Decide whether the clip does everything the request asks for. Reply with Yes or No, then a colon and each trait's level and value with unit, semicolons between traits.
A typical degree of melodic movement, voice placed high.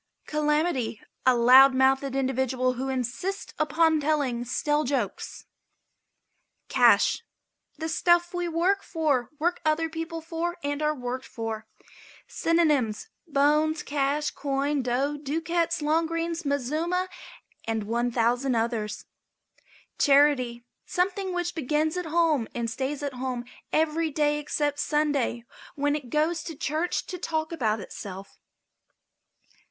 Yes: average, 4.3 semitones; very high, 295 Hz